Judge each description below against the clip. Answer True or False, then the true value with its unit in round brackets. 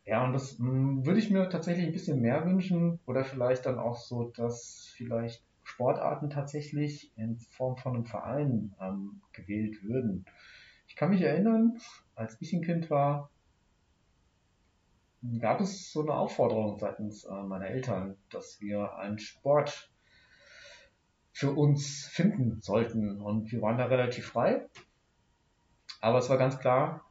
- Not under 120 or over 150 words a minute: True (140 wpm)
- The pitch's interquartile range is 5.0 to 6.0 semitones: True (5.3 semitones)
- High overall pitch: False (125 Hz)